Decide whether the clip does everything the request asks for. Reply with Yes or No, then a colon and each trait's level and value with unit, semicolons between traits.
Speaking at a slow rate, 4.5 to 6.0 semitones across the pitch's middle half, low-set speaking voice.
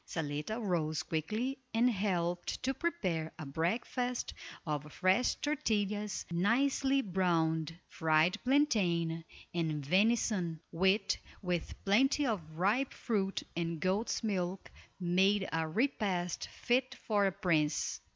No: slow, 110 wpm; wide, 5.4 semitones; high, 190 Hz